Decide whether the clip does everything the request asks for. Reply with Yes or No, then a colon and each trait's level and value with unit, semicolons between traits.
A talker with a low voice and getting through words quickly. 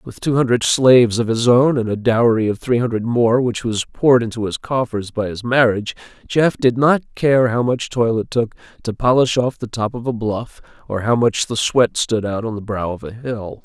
Yes: low, 115 Hz; fast, 235 wpm